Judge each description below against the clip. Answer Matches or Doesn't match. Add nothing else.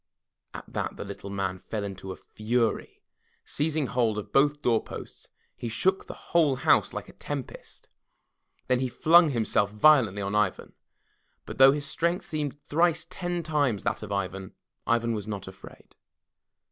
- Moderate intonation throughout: Doesn't match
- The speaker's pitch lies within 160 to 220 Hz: Doesn't match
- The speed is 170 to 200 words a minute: Doesn't match